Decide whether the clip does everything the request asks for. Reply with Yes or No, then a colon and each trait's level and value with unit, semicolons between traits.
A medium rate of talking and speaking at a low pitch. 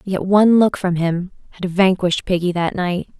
No: average, 190 wpm; medium, 185 Hz